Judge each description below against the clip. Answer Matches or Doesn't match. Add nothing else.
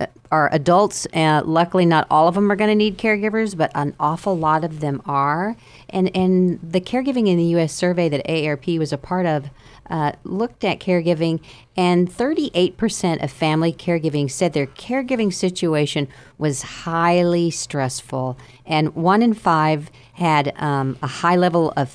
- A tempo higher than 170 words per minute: Doesn't match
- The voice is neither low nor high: Matches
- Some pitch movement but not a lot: Matches